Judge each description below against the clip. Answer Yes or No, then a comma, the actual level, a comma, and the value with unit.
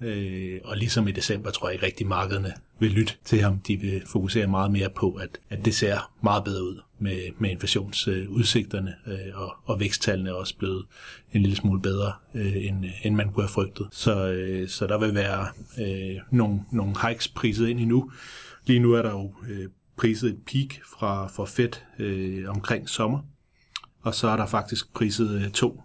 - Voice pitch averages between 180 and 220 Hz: No, low, 105 Hz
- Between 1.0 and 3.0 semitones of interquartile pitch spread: Yes, average, 2.7 semitones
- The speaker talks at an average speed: Yes, average, 195 wpm